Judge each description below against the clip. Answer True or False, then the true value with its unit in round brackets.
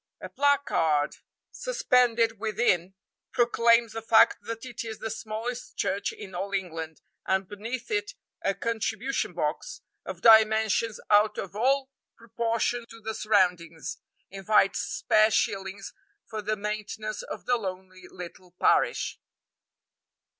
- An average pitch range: True (3.1 semitones)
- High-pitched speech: True (220 Hz)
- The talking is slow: True (125 wpm)